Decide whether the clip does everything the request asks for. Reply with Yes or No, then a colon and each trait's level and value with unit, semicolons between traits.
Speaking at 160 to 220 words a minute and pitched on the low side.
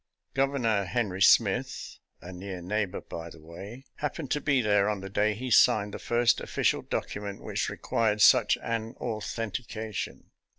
Yes: average, 165 wpm; low, 105 Hz